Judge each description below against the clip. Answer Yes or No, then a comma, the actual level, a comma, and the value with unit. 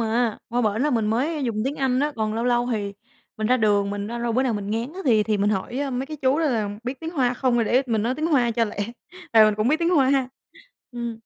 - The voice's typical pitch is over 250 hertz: No, high, 240 Hz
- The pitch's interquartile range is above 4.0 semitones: No, average, 3.5 semitones